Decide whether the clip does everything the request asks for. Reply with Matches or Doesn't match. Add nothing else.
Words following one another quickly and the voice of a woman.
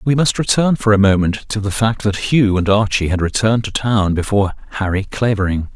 Doesn't match